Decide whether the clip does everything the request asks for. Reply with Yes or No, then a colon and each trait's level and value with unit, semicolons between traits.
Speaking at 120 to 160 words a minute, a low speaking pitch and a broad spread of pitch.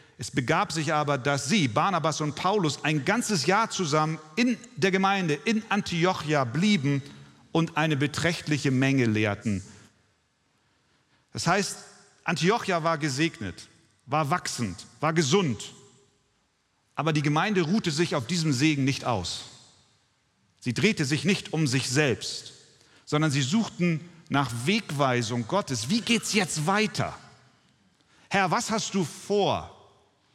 No: average, 130 wpm; medium, 155 Hz; wide, 5.8 semitones